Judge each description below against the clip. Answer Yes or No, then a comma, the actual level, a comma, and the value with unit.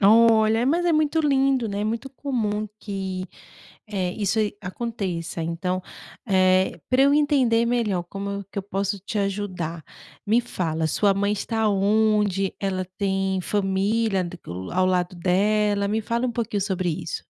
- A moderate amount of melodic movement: Yes, average, 3.3 semitones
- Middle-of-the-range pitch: No, high, 205 Hz